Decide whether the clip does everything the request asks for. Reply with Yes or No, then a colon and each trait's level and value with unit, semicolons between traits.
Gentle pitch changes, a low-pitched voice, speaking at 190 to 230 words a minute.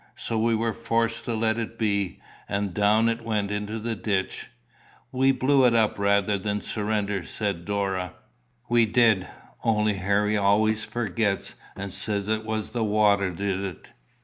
No: narrow, 2.0 semitones; low, 105 Hz; average, 160 wpm